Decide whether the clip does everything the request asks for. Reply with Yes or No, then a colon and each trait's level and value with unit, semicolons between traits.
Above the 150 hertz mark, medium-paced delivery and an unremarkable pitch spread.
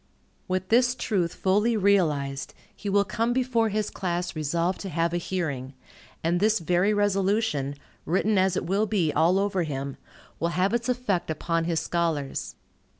Yes: medium, 185 Hz; average, 160 wpm; average, 3.8 semitones